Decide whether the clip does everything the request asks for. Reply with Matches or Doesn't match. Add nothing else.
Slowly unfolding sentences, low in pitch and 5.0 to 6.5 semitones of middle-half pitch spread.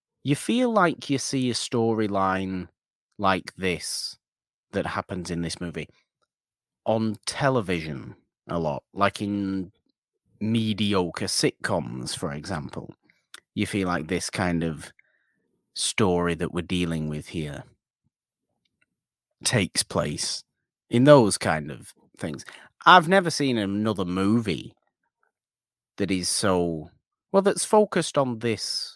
Matches